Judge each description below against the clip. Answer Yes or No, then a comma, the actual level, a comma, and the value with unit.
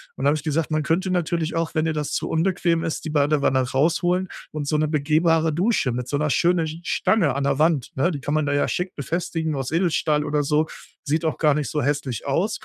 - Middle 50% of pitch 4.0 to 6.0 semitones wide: No, narrow, 2.4 semitones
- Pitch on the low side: No, medium, 155 Hz